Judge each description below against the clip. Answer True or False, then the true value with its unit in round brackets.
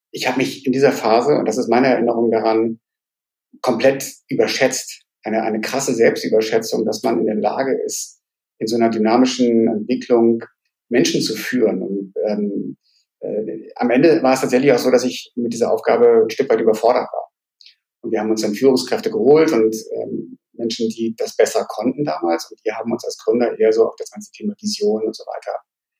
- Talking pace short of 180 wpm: False (190 wpm)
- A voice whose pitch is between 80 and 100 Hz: False (125 Hz)